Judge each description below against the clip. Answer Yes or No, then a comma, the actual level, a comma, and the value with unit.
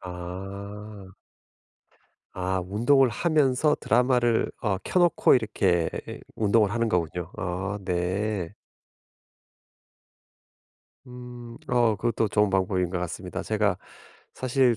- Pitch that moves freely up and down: No, average, 4.5 semitones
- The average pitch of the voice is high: No, low, 105 Hz